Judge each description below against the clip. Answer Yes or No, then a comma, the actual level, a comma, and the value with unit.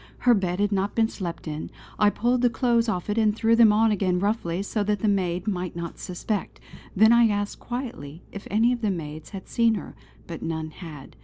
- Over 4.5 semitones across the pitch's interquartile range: No, average, 4.1 semitones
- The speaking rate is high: Yes, fast, 220 wpm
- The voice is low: No, high, 205 Hz